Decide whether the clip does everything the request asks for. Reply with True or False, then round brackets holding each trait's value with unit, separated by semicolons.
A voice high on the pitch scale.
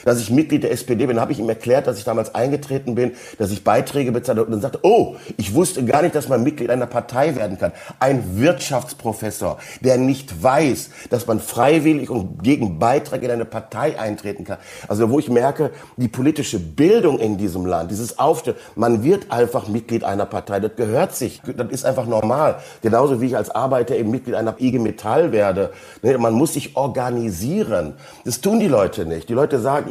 False (120 Hz)